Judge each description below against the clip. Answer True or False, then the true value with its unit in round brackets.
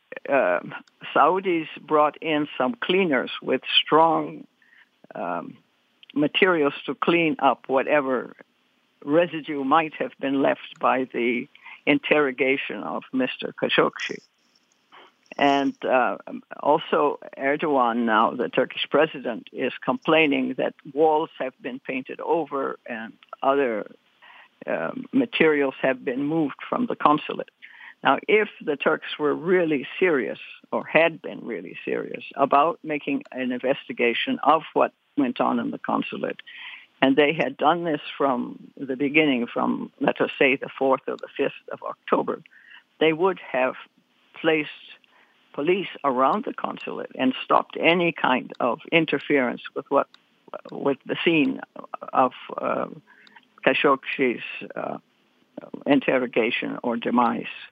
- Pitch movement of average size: True (5.0 semitones)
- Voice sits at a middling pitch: True (150 Hz)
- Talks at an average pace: False (125 wpm)